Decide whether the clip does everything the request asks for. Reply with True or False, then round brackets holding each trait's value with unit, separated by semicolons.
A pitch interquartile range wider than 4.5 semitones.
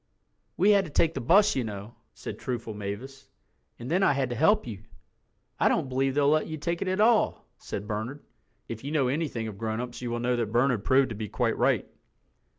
True (5.4 semitones)